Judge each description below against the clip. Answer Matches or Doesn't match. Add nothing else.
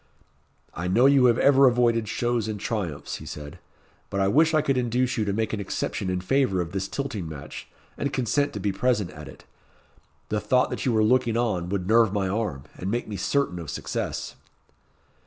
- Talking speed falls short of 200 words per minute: Doesn't match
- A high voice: Doesn't match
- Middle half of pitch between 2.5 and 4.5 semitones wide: Doesn't match